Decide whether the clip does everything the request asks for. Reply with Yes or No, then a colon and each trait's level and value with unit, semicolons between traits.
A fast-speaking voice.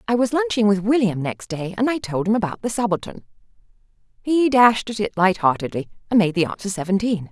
No: average, 195 wpm